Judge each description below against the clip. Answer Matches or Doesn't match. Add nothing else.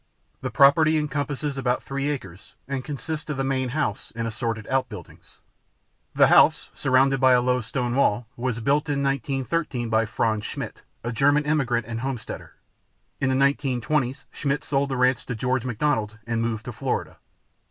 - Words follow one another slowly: Doesn't match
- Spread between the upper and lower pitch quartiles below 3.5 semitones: Matches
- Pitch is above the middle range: Doesn't match